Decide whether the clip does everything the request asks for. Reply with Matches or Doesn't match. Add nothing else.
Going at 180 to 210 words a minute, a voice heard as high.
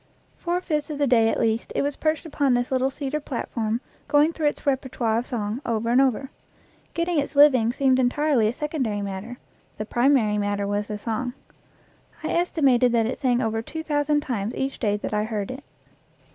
Matches